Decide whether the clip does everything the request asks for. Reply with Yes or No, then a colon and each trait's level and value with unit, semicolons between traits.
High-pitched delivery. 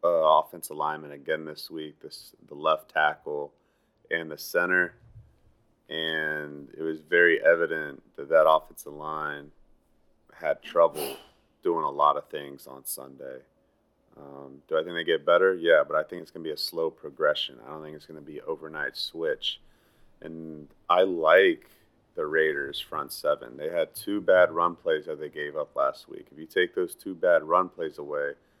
No: very low, 80 Hz